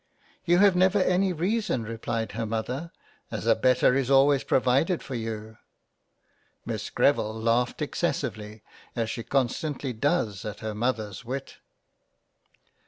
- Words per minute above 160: No, average, 140 wpm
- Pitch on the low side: Yes, low, 125 Hz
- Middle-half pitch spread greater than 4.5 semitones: Yes, wide, 5.4 semitones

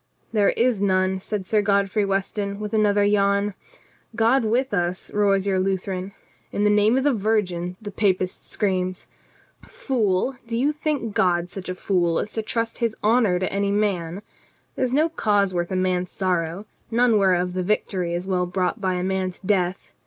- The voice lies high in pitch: Yes, high, 200 Hz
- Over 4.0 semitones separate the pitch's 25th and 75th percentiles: No, average, 2.7 semitones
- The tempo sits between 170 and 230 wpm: Yes, average, 190 wpm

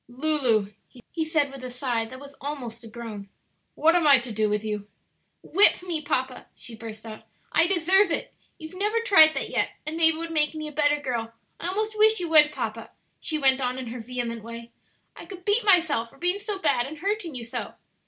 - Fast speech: Yes, fast, 220 wpm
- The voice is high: Yes, very high, 290 Hz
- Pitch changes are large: Yes, wide, 6.1 semitones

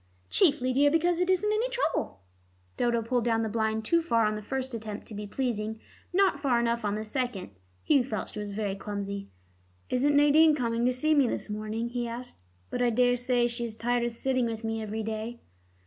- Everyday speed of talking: No, fast, 210 wpm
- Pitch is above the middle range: Yes, high, 235 Hz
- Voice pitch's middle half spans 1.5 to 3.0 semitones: No, average, 3.5 semitones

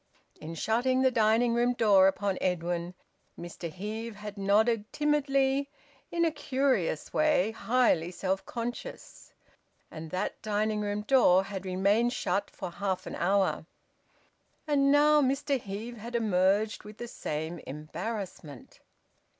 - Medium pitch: No, high, 210 Hz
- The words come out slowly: Yes, slow, 130 wpm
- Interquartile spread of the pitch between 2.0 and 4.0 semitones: No, average, 4.7 semitones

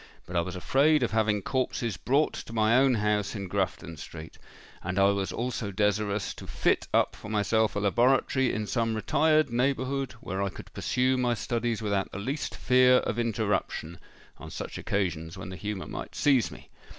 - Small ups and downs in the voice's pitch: No, average, 4.3 semitones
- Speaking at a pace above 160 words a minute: Yes, average, 185 wpm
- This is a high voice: No, low, 110 Hz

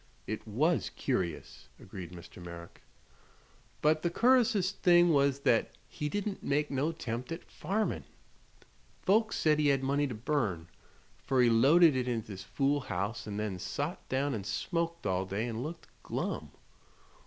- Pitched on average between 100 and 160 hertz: Yes, low, 135 Hz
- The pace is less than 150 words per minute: No, average, 155 wpm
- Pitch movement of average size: No, wide, 7.4 semitones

